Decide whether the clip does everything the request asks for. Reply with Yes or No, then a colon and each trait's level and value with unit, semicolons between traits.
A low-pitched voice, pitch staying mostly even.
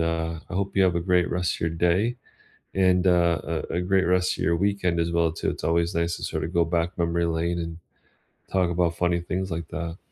Yes: very low, 85 Hz; narrow, 1.5 semitones